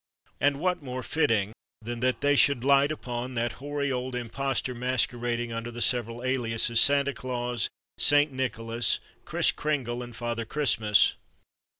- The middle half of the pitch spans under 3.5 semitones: Yes, average, 2.8 semitones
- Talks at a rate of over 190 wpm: No, average, 140 wpm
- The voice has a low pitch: Yes, low, 125 Hz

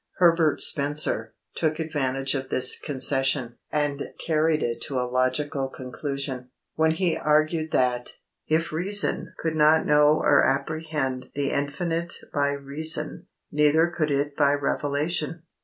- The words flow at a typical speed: No, slow, 130 wpm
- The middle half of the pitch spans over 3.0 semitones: No, average, 2.7 semitones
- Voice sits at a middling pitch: Yes, medium, 145 Hz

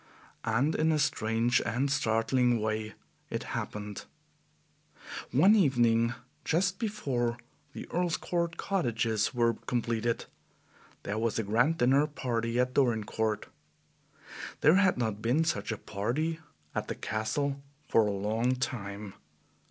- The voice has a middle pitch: No, low, 120 Hz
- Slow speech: Yes, slow, 125 wpm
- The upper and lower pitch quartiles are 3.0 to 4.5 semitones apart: No, average, 4.9 semitones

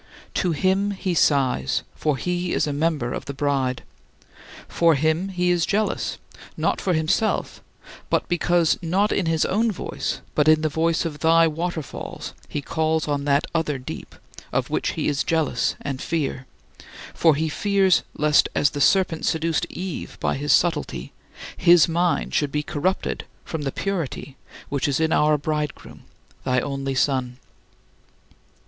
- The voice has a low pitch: No, medium, 160 Hz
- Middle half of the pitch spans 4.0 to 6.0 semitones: No, average, 3.4 semitones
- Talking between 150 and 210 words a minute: Yes, average, 160 wpm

